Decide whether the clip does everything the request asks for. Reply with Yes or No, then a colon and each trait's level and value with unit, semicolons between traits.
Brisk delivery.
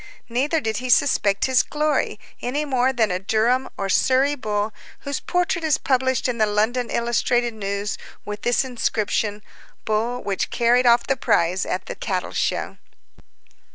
No: average, 155 wpm